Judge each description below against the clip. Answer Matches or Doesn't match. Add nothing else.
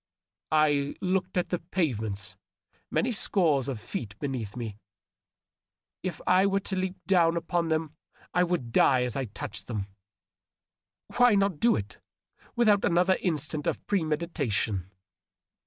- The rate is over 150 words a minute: Doesn't match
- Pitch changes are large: Matches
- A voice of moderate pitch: Matches